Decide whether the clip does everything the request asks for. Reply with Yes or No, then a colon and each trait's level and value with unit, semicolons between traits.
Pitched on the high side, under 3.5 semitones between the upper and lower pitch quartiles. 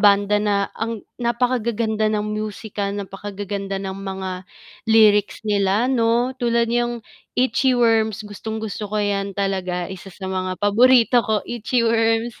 Yes: high, 215 Hz; narrow, 2.6 semitones